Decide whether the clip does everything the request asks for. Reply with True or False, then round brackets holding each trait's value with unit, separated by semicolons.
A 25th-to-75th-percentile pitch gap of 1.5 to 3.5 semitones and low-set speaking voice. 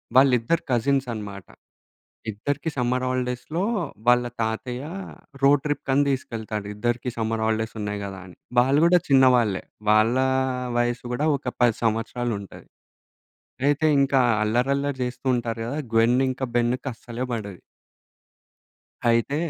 True (3.0 semitones; 120 Hz)